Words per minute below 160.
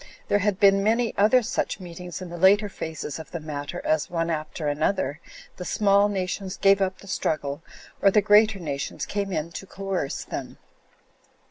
No: average, 175 wpm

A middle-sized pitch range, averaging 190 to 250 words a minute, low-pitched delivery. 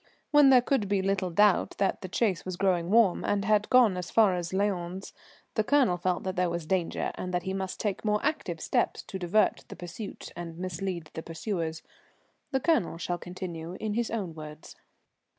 No: average, 3.3 semitones; average, 195 wpm; medium, 185 Hz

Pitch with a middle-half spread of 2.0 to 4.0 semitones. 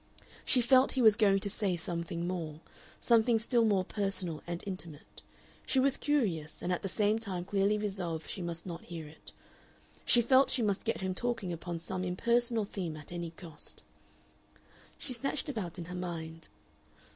No: average, 4.7 semitones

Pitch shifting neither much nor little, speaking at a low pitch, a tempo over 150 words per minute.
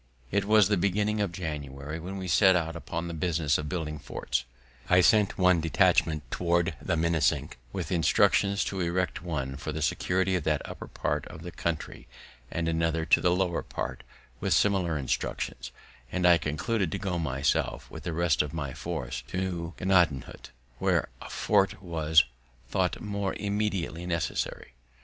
Yes: average, 3.1 semitones; very low, 85 Hz; average, 165 wpm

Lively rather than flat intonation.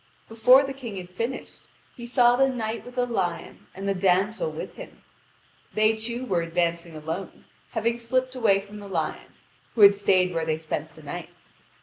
No: average, 5.0 semitones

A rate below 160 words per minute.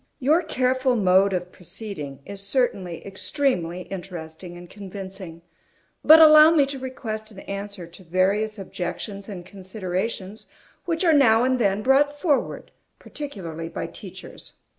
Yes: slow, 135 wpm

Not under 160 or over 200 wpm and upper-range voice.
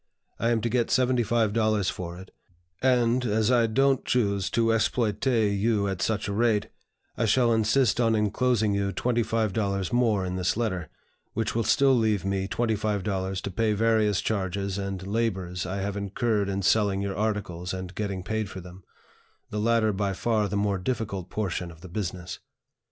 No: average, 170 wpm; low, 105 Hz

